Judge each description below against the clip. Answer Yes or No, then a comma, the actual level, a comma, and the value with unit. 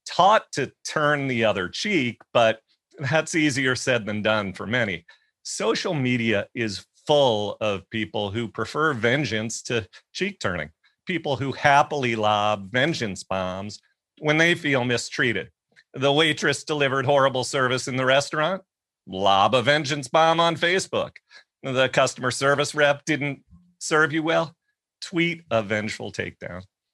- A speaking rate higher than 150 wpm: No, average, 140 wpm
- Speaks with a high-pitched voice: No, low, 135 Hz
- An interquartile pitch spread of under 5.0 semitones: No, wide, 5.6 semitones